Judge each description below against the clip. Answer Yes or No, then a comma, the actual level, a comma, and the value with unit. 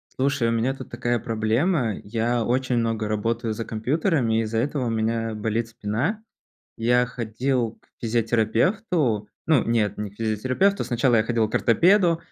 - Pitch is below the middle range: Yes, low, 115 Hz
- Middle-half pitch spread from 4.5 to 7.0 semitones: No, average, 2.8 semitones